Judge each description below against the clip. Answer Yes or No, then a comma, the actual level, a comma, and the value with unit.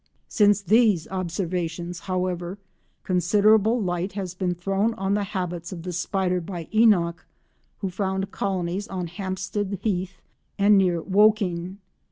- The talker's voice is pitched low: No, medium, 185 Hz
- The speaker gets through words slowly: Yes, slow, 130 wpm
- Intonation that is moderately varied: No, narrow, 2.3 semitones